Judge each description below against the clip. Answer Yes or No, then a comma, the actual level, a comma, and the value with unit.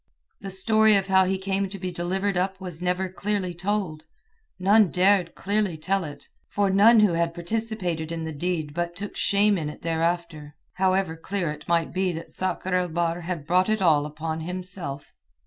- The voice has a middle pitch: Yes, medium, 180 Hz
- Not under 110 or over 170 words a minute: No, average, 185 wpm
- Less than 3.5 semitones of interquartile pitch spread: Yes, average, 2.8 semitones